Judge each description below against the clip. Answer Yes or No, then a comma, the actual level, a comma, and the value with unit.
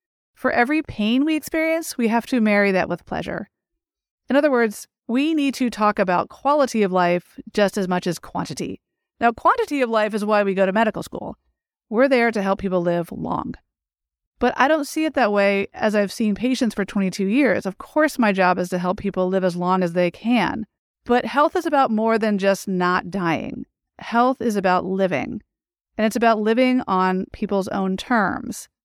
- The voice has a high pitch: Yes, high, 215 Hz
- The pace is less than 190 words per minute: No, average, 200 wpm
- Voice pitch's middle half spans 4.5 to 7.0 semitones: Yes, average, 5.2 semitones